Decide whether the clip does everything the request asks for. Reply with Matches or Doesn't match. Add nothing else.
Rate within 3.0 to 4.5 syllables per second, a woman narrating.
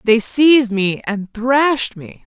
Matches